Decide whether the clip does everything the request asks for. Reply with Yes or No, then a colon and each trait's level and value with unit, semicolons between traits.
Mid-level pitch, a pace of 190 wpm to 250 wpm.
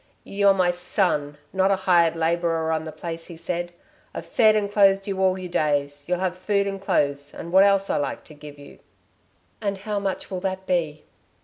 Yes: medium, 180 Hz; fast, 205 wpm